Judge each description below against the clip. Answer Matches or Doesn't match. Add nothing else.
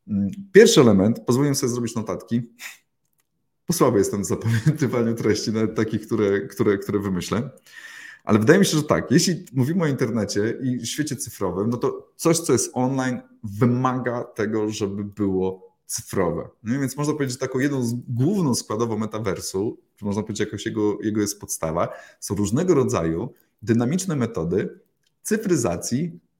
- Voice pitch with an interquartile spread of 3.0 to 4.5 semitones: Matches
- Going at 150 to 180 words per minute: Matches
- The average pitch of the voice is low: Matches